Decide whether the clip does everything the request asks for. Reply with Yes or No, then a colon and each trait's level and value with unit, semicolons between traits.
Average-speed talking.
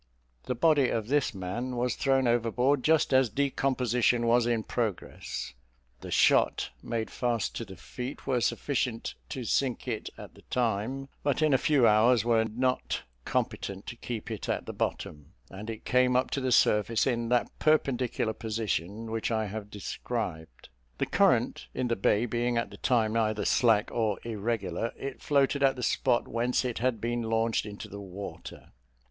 Yes: average, 175 wpm